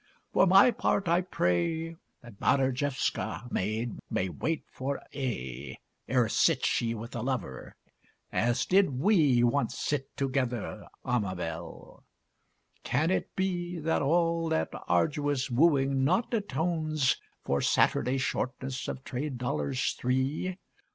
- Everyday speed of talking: No, slow, 120 wpm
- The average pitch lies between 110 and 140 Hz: Yes, low, 135 Hz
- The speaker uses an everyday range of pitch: Yes, average, 5.0 semitones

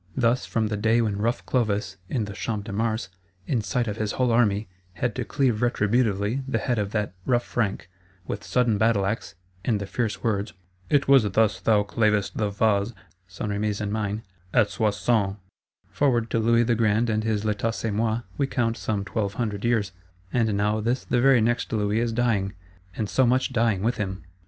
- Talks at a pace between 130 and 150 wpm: No, average, 195 wpm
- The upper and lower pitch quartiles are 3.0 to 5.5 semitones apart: No, narrow, 2.4 semitones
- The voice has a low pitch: Yes, low, 110 Hz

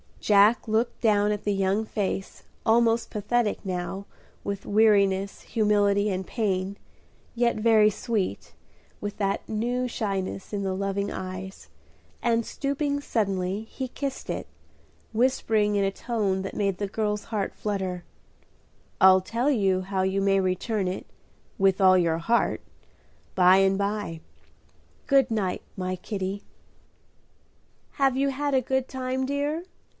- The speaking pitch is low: No, high, 205 Hz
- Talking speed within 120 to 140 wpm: Yes, slow, 135 wpm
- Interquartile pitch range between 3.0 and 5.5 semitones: Yes, average, 3.3 semitones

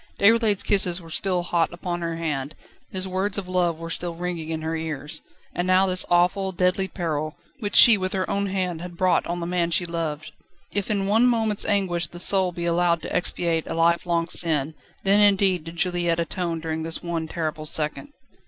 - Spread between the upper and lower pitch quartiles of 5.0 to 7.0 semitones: No, narrow, 2.4 semitones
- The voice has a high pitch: No, medium, 175 Hz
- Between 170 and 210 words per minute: Yes, average, 200 wpm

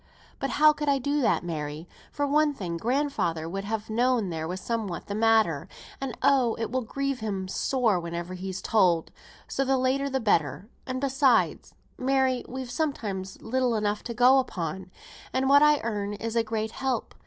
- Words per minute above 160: Yes, average, 180 wpm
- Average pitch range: No, wide, 5.8 semitones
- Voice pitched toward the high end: Yes, high, 230 Hz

